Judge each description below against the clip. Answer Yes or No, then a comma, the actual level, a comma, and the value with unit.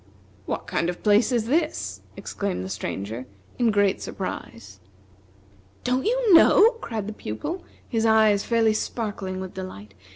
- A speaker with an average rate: Yes, average, 150 wpm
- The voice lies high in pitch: Yes, high, 215 Hz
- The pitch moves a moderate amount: Yes, average, 4.5 semitones